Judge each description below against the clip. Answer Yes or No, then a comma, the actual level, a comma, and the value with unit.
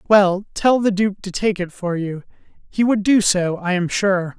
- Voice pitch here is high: Yes, high, 195 Hz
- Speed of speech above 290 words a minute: No, fast, 220 wpm